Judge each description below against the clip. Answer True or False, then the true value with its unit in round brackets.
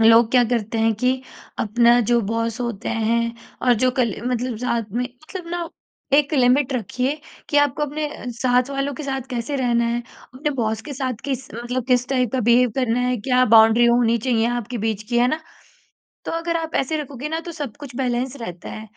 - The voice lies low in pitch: False (245 Hz)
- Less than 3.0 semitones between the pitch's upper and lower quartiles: True (2.5 semitones)